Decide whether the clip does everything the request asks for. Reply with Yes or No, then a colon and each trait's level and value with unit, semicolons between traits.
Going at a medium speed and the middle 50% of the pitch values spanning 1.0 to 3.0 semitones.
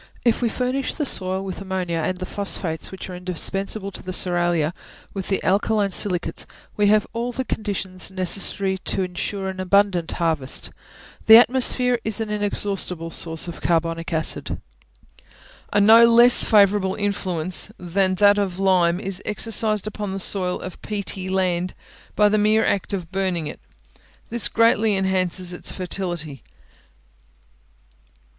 Yes: average, 145 wpm; narrow, 2.5 semitones